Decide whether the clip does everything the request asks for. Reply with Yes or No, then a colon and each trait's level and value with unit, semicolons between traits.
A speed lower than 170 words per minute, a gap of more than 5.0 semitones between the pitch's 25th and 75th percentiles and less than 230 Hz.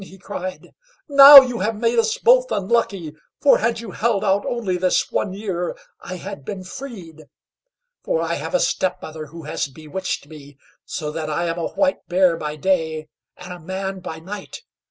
No: average, 185 wpm; wide, 5.5 semitones; medium, 185 Hz